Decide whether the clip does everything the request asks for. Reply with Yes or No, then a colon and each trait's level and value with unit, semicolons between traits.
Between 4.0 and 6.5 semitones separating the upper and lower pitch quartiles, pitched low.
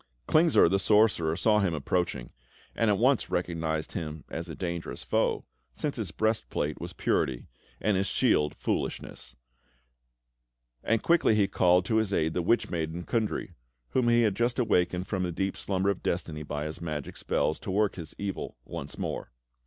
Yes: average, 4.8 semitones; very low, 95 Hz